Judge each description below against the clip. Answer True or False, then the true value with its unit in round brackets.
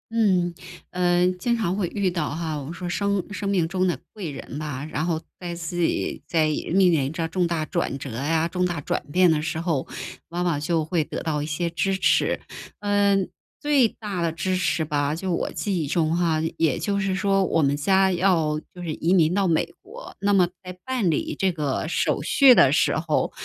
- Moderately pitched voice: True (175 Hz)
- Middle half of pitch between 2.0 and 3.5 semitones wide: True (3.2 semitones)